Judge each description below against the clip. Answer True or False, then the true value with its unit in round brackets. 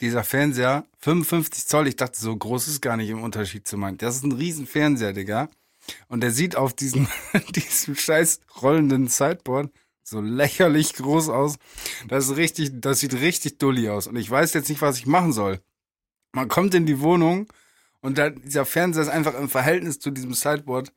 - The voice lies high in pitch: False (140 Hz)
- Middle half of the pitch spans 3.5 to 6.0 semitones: True (4.1 semitones)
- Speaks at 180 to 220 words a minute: True (190 wpm)